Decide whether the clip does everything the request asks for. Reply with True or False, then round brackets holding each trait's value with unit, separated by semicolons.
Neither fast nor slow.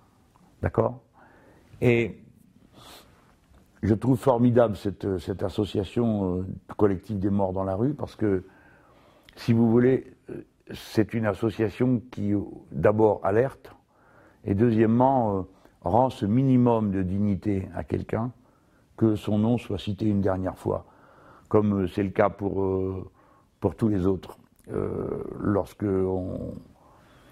False (125 wpm)